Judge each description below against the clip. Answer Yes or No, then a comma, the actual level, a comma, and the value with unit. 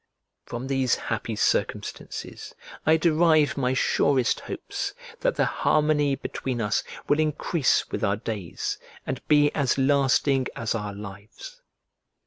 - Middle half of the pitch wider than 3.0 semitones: Yes, average, 4.3 semitones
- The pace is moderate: No, slow, 125 wpm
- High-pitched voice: No, low, 135 Hz